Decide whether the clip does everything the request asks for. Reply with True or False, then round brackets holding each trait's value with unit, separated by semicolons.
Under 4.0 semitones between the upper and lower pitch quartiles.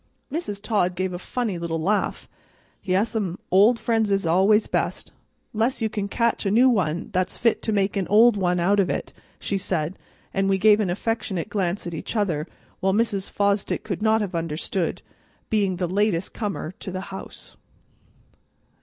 True (3.0 semitones)